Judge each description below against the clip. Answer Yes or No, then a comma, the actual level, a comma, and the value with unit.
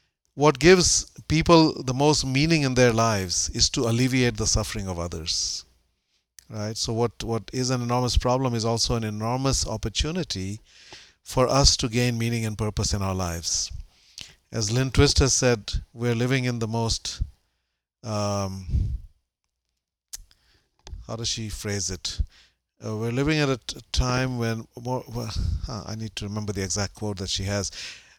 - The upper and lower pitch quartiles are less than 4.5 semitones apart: No, average, 5.0 semitones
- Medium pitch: No, low, 110 Hz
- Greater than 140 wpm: Yes, average, 160 wpm